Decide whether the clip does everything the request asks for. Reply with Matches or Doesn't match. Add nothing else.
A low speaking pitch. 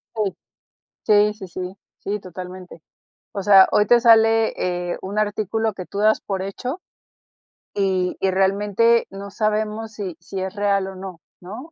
Doesn't match